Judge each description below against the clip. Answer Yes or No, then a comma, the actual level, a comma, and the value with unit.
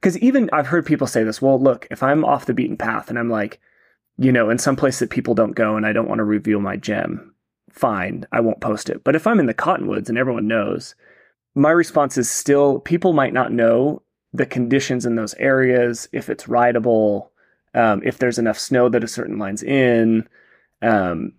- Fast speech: Yes, fast, 215 wpm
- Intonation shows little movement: No, average, 3.4 semitones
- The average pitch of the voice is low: Yes, low, 120 Hz